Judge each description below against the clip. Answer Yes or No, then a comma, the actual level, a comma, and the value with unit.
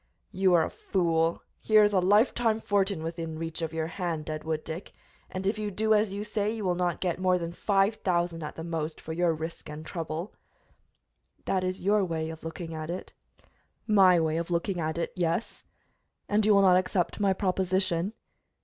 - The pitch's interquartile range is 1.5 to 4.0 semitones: Yes, average, 3.3 semitones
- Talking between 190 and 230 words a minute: Yes, average, 200 wpm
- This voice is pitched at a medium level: Yes, medium, 180 Hz